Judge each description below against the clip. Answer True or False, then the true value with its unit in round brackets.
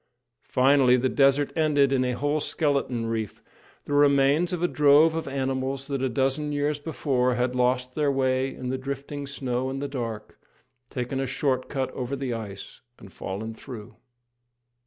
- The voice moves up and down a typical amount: False (2.2 semitones)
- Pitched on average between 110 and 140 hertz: True (135 Hz)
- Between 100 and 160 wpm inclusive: False (170 wpm)